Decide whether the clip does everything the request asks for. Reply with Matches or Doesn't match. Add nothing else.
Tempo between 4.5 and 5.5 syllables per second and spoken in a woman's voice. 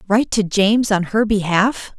Matches